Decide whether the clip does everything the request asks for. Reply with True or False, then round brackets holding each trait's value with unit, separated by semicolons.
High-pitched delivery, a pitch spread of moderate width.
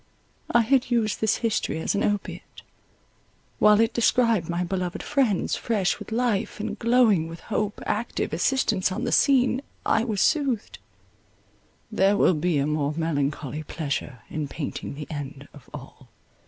False (195 Hz; 6.8 semitones)